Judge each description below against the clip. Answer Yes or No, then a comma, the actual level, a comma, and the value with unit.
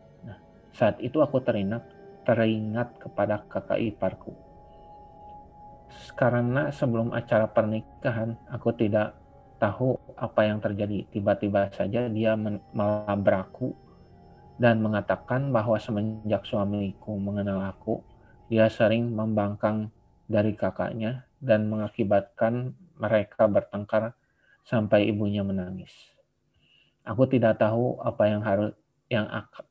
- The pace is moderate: Yes, average, 100 wpm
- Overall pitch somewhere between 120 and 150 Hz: No, low, 110 Hz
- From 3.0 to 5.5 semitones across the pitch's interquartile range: No, narrow, 2.4 semitones